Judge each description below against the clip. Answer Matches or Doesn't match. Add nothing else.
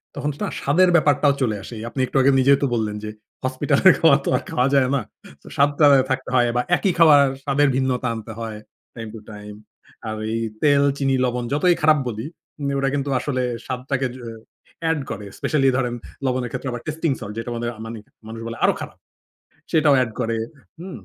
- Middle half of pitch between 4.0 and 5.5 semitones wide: Doesn't match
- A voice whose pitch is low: Matches